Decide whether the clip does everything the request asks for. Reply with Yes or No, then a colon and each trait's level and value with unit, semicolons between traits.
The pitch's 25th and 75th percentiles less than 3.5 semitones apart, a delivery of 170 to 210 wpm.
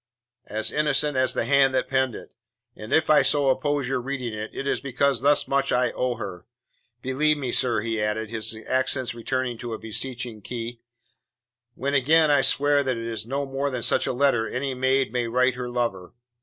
Yes: average, 3.0 semitones; average, 200 wpm